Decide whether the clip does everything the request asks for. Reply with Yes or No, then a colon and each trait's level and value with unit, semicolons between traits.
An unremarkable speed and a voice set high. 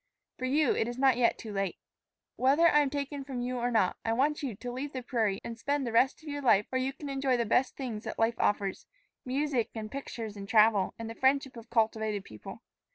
No: fast, 235 wpm; high, 245 Hz